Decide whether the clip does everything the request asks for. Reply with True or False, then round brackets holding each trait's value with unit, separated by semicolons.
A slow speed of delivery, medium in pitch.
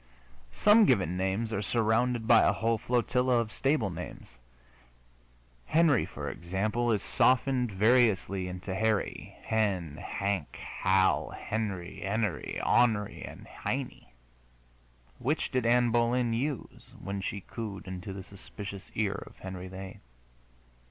False (125 wpm; 110 Hz)